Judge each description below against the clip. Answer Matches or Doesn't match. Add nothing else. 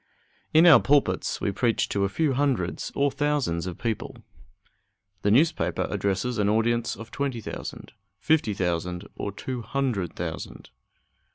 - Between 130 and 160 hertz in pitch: Doesn't match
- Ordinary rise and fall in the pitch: Doesn't match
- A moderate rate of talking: Matches